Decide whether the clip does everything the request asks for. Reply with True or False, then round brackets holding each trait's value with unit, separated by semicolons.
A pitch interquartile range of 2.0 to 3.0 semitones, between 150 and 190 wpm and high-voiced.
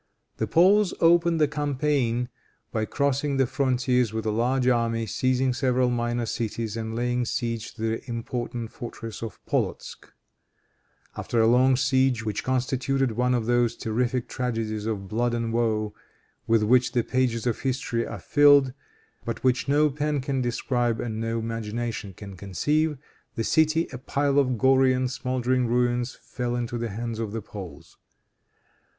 False (2.5 semitones; 155 wpm; 120 Hz)